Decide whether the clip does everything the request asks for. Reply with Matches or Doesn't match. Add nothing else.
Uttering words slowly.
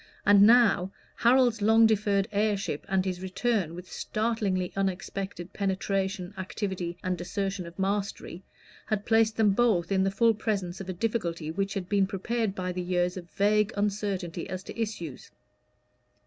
Doesn't match